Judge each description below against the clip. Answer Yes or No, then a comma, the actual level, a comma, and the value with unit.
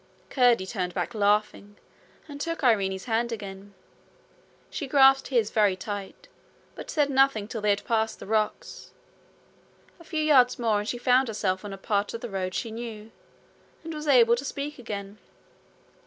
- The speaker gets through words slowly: No, average, 170 wpm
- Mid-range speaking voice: No, high, 225 Hz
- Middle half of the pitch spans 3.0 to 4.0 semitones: No, average, 4.4 semitones